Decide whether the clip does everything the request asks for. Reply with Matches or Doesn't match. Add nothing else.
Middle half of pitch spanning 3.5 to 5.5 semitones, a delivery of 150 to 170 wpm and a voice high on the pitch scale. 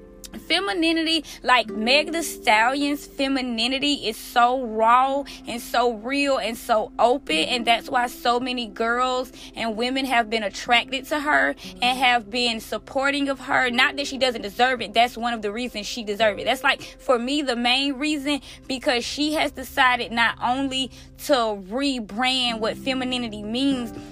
Doesn't match